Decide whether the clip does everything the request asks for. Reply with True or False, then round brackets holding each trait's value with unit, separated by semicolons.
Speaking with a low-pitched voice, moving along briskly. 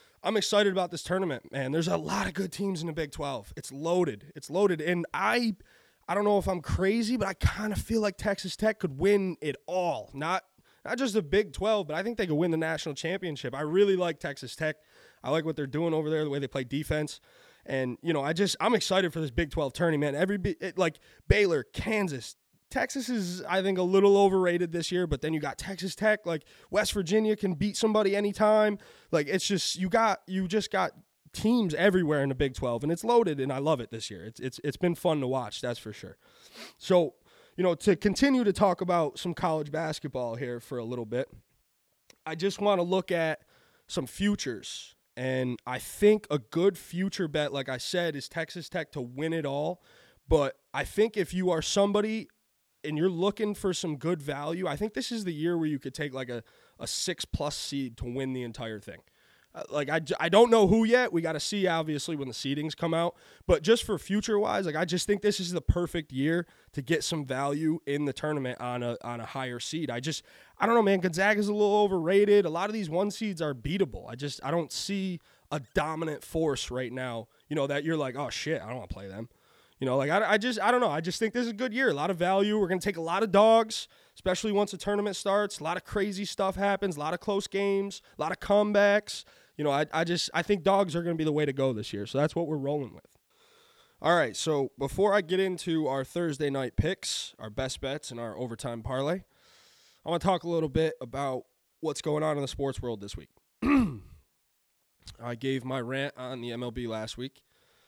False (170 Hz; 235 wpm)